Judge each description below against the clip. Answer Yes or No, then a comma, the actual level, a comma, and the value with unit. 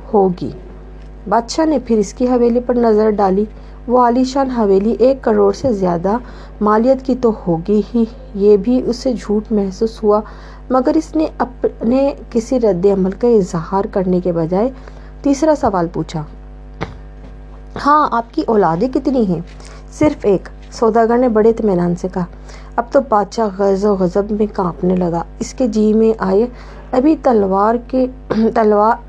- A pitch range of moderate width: Yes, average, 3.9 semitones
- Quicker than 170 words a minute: No, average, 155 wpm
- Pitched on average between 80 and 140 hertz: No, high, 220 Hz